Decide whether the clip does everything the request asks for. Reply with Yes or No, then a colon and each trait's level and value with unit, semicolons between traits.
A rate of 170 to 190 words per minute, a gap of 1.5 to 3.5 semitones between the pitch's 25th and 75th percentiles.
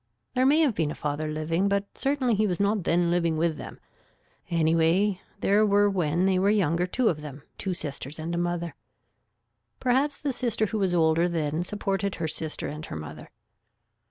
No: average, 185 wpm; average, 4.3 semitones